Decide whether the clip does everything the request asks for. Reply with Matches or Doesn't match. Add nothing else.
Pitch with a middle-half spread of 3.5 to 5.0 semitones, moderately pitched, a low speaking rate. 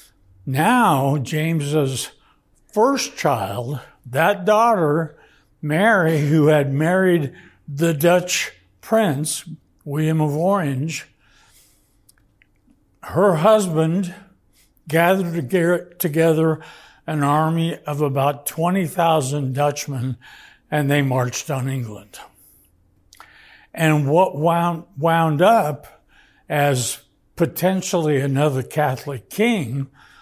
Matches